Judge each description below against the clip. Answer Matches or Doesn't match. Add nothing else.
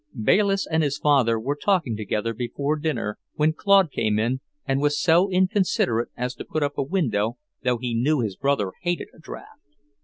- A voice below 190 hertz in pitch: Matches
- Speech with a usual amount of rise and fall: Doesn't match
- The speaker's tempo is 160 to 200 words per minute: Matches